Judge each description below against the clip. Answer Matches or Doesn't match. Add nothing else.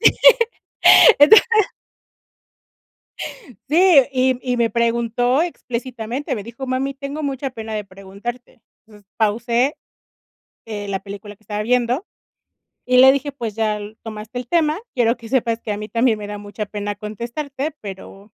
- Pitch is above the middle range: Matches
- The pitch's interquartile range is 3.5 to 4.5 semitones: Matches